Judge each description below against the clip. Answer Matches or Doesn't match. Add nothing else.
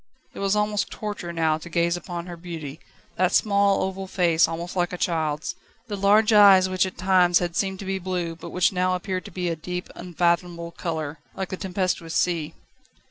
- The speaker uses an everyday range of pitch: Doesn't match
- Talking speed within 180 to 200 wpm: Matches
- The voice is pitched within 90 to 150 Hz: Doesn't match